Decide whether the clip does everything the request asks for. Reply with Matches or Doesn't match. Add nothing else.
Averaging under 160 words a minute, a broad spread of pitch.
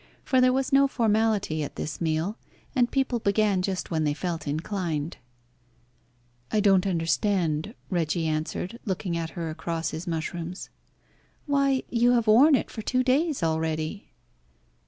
Matches